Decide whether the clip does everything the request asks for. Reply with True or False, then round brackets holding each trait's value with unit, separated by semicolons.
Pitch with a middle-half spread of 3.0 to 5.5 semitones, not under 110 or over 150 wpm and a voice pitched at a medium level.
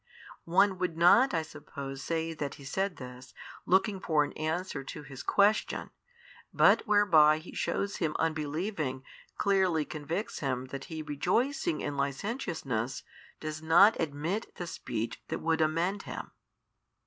True (4.9 semitones; 140 wpm; 160 Hz)